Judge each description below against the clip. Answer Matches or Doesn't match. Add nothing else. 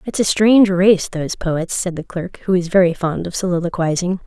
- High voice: Doesn't match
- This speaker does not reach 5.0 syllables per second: Doesn't match